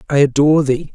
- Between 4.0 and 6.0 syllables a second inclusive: No, 6.5 syllables/s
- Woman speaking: Yes, female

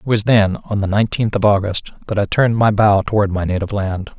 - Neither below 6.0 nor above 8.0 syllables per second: Yes, 6.1 syllables/s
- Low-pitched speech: Yes, low, 105 Hz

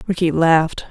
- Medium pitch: Yes, medium, 165 Hz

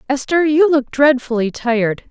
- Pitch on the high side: Yes, very high, 265 Hz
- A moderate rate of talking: Yes, average, 145 wpm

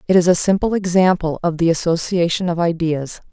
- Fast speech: No, average, 180 wpm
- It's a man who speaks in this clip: No, female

